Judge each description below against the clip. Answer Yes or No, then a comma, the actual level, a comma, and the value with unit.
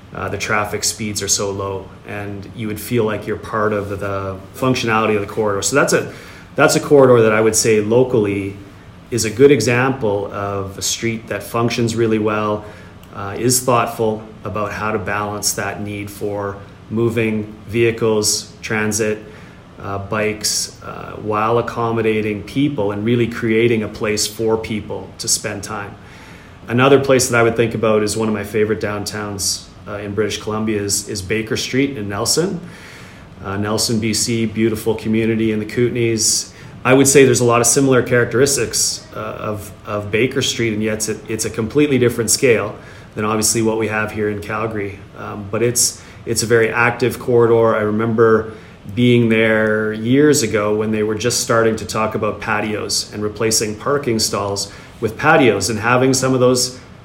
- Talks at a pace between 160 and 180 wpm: Yes, average, 175 wpm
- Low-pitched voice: Yes, low, 110 Hz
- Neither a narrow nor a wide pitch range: No, narrow, 2.1 semitones